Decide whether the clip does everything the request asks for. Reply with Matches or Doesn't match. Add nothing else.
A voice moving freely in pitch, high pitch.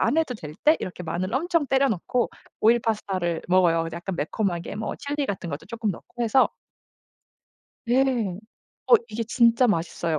Matches